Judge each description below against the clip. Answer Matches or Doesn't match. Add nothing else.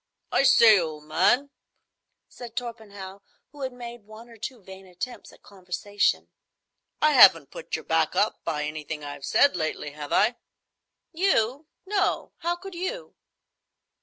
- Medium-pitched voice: Doesn't match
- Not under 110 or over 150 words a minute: Matches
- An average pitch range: Doesn't match